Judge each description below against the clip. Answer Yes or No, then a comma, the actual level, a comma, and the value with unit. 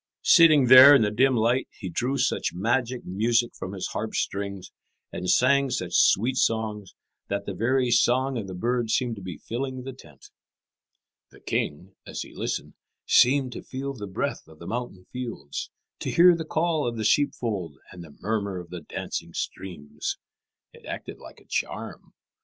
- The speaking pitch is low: Yes, low, 115 Hz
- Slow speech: No, average, 175 wpm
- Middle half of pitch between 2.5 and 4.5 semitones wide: No, average, 5.3 semitones